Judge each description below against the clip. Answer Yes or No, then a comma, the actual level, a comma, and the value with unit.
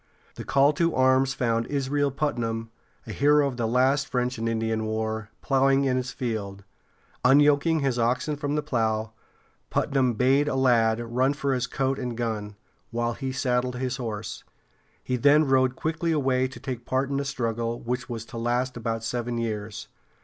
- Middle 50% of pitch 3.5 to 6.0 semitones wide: No, average, 3.0 semitones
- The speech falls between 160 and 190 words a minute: Yes, average, 175 wpm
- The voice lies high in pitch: No, low, 125 Hz